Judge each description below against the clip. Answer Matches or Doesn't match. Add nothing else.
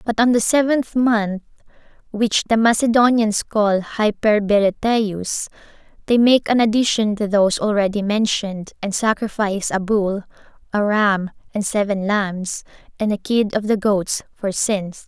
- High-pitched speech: Matches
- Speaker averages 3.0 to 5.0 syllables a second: Matches